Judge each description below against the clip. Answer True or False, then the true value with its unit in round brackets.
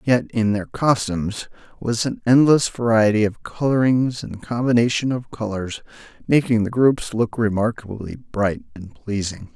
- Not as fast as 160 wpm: True (140 wpm)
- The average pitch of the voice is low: True (115 Hz)